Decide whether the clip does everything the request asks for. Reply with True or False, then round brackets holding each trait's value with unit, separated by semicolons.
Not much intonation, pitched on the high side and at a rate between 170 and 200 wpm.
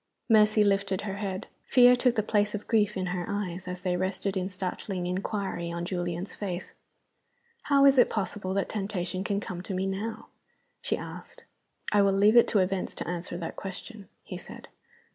True (2.3 semitones; 195 Hz; 185 wpm)